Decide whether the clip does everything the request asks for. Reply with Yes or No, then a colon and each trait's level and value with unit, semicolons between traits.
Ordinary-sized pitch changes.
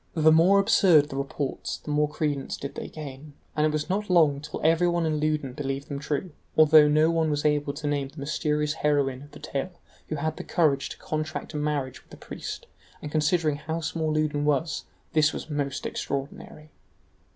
No: narrow, 1.5 semitones